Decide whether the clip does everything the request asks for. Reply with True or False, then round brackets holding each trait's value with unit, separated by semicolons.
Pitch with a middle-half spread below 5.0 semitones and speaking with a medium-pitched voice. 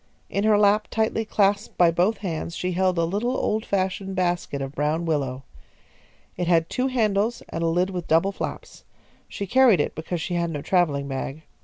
True (3.8 semitones; 180 Hz)